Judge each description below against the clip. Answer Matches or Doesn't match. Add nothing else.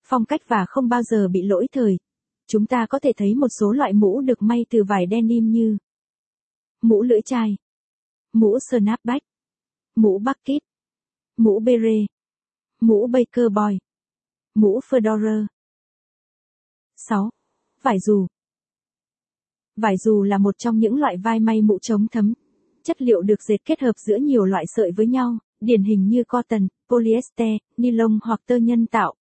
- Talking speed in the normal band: Doesn't match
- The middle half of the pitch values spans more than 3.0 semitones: Doesn't match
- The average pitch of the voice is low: Doesn't match